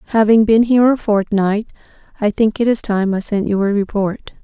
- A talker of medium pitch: No, high, 210 Hz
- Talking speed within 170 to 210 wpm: Yes, fast, 205 wpm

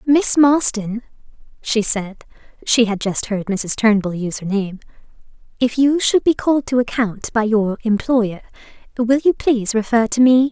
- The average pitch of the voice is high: Yes, high, 230 Hz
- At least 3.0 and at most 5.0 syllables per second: Yes, 4.7 syllables/s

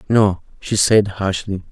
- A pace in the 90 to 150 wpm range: Yes, average, 140 wpm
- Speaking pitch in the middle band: No, low, 100 Hz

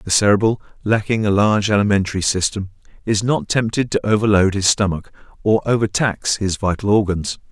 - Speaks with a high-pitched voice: No, low, 105 Hz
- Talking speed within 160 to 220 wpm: No, average, 150 wpm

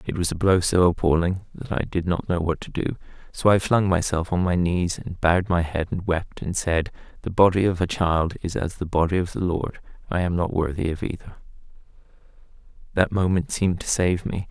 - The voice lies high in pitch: No, very low, 90 Hz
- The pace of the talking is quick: Yes, fast, 220 wpm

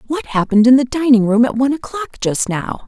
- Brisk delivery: Yes, fast, 230 wpm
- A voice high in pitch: Yes, very high, 250 Hz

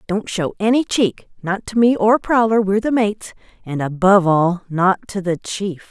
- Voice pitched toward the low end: No, high, 200 Hz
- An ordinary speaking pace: Yes, average, 175 wpm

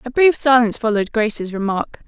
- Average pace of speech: Yes, average, 175 wpm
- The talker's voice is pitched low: No, high, 230 Hz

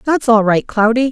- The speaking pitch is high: Yes, high, 235 Hz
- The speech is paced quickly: Yes, fast, 215 wpm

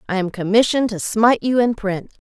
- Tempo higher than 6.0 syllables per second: Yes, 6.2 syllables/s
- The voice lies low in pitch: No, high, 215 Hz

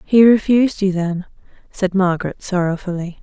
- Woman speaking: Yes, female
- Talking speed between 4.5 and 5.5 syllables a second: Yes, 5.3 syllables/s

